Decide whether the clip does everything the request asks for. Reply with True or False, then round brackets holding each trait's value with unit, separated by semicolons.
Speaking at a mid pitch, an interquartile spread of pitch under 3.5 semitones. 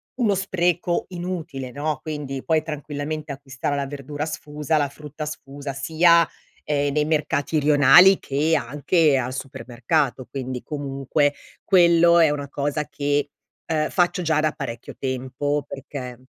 True (145 Hz; 2.5 semitones)